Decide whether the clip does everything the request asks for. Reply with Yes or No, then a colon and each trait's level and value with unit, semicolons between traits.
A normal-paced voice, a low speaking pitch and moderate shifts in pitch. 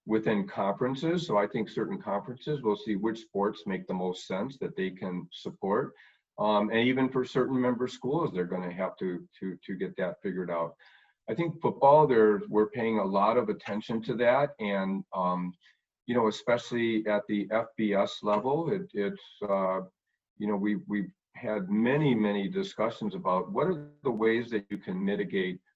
Yes: average, 180 wpm; low, 105 Hz; average, 4.4 semitones